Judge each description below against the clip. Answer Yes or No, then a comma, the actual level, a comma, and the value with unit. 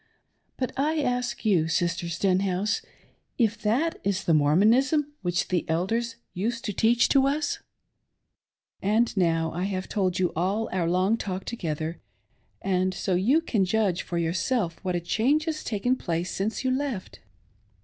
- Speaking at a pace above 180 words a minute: No, average, 150 wpm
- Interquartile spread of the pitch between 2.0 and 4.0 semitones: No, average, 5.2 semitones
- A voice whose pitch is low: No, high, 195 Hz